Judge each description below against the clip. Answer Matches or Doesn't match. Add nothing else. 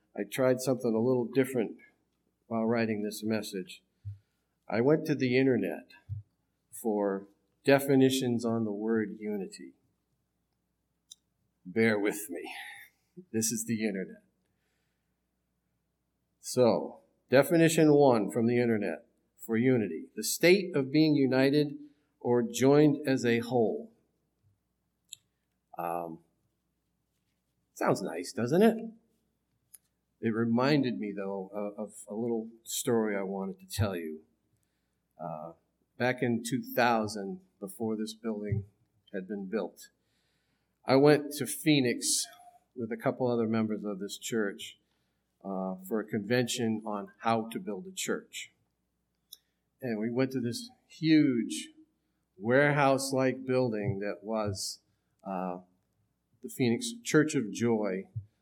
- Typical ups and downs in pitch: Matches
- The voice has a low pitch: Matches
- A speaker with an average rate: Doesn't match